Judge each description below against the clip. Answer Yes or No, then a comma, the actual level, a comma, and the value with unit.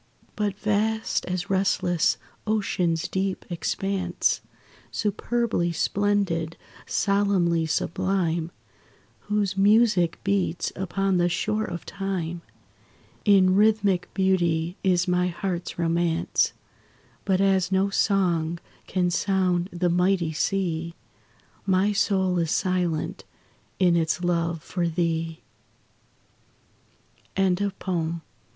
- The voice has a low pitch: No, medium, 185 Hz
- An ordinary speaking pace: No, slow, 100 wpm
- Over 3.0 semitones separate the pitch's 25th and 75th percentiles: No, narrow, 2.4 semitones